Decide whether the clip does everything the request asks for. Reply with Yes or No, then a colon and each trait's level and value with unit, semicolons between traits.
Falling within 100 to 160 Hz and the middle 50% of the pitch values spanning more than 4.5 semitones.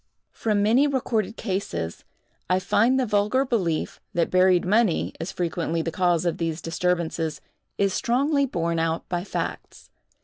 No: medium, 185 Hz; average, 5.0 semitones